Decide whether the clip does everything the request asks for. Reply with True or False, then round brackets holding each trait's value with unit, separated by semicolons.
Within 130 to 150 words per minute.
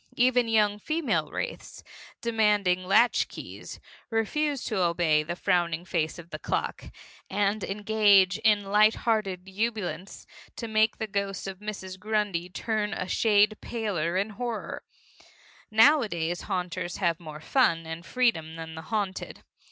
True (135 wpm)